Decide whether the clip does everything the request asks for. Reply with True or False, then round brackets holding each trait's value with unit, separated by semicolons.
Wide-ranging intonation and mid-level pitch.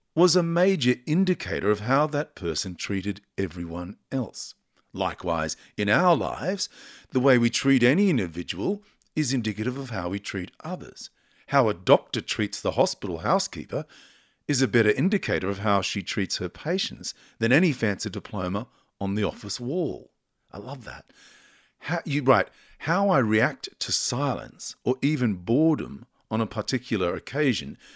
False (6.6 semitones; 115 Hz)